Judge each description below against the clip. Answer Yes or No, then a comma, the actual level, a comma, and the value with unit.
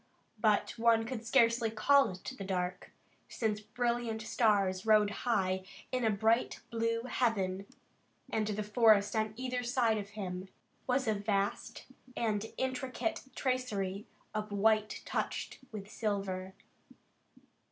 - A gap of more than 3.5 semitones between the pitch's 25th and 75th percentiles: No, average, 2.8 semitones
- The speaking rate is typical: No, slow, 125 wpm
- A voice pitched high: Yes, high, 215 Hz